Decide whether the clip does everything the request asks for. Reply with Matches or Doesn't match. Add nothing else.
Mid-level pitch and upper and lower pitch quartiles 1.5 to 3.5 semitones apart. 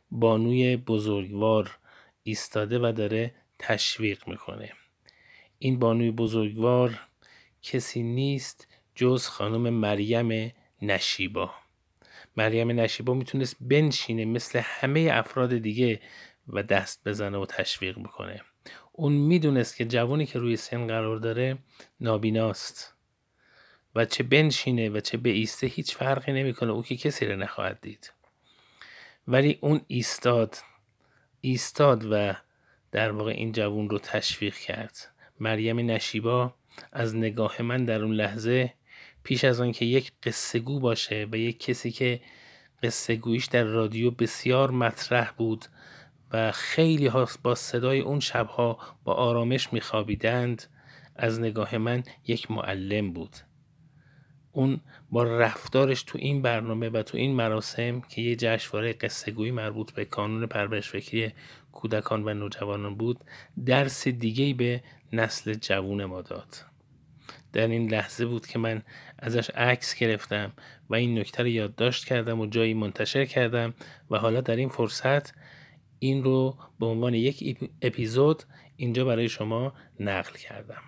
Doesn't match